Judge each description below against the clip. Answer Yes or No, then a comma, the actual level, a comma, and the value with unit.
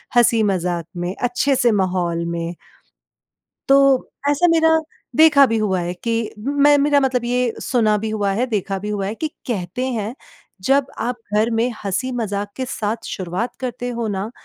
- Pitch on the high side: Yes, high, 230 Hz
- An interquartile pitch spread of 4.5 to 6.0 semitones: Yes, average, 4.8 semitones